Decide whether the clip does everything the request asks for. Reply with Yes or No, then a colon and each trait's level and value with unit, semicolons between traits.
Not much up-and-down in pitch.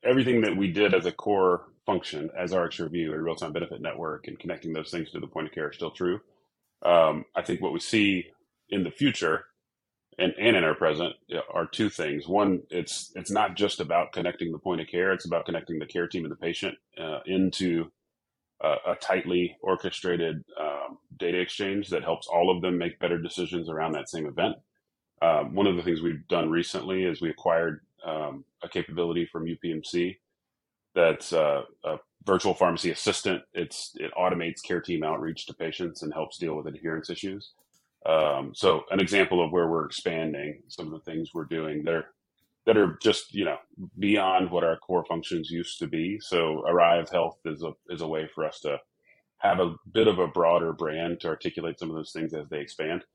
Yes: narrow, 2.1 semitones